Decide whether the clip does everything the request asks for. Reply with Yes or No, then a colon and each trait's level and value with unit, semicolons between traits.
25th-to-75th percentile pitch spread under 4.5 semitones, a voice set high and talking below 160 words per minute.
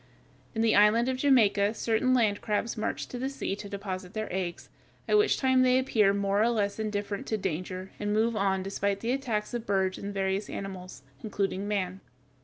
No: average, 2.8 semitones; high, 205 Hz; average, 195 wpm